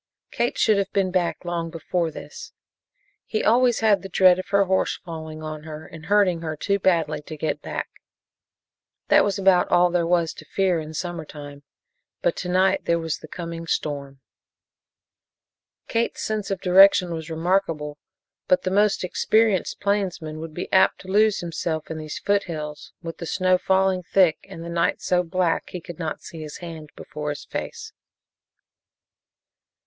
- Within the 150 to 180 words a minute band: Yes, average, 170 wpm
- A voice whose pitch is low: No, medium, 175 Hz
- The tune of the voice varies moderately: Yes, average, 3.3 semitones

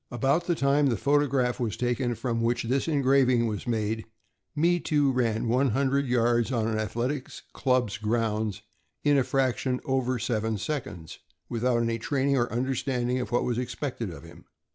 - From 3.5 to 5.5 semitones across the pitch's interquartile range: No, average, 2.8 semitones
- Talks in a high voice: No, low, 125 Hz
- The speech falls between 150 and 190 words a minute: Yes, average, 165 wpm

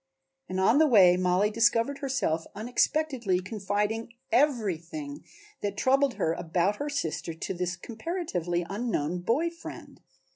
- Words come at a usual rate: No, slow, 125 wpm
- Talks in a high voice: Yes, high, 210 Hz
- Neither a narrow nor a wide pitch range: No, wide, 7.0 semitones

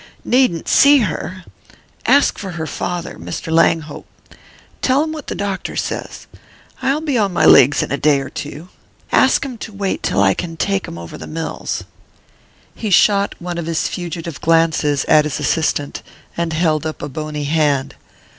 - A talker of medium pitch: Yes, medium, 165 Hz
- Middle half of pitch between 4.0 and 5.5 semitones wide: Yes, average, 4.6 semitones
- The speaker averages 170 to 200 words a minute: Yes, average, 175 wpm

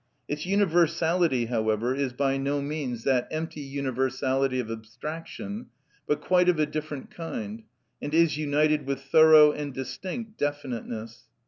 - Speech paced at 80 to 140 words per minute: Yes, slow, 135 wpm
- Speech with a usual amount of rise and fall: Yes, average, 3.6 semitones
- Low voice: No, medium, 145 Hz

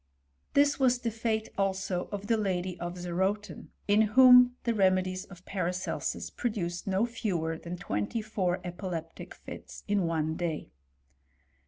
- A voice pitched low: No, high, 190 Hz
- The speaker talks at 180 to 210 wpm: No, average, 140 wpm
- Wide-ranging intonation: No, average, 3.8 semitones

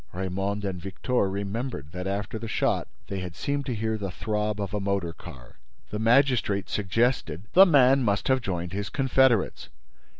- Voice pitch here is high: No, low, 100 Hz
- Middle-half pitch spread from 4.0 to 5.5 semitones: Yes, average, 4.3 semitones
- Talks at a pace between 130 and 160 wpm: No, average, 170 wpm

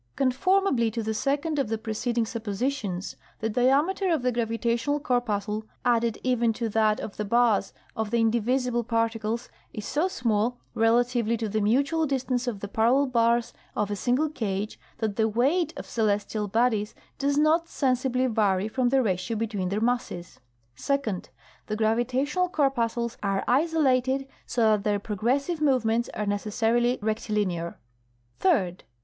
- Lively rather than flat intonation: No, average, 3.3 semitones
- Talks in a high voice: Yes, high, 235 Hz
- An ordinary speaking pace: Yes, average, 150 wpm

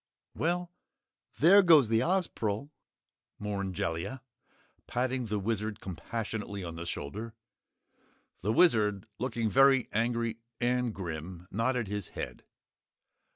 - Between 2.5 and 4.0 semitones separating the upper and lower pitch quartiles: No, average, 4.4 semitones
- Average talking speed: No, slow, 110 wpm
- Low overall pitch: Yes, low, 110 Hz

